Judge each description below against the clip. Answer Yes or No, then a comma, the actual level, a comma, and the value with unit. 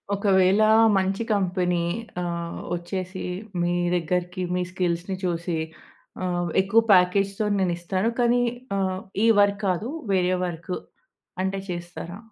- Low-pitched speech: No, medium, 185 Hz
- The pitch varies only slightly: Yes, narrow, 1.9 semitones